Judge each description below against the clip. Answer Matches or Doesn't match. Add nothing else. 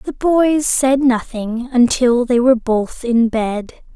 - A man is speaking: Doesn't match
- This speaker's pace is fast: Doesn't match